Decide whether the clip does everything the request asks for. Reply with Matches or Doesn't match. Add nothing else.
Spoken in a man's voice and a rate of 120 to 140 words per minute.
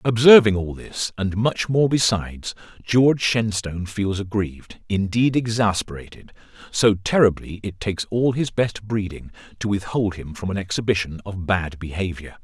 Matches